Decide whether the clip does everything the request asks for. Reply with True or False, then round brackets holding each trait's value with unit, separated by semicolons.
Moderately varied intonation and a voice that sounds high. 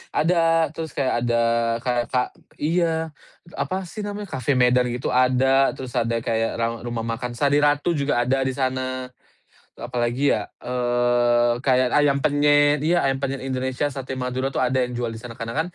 False (3.1 semitones; 130 Hz)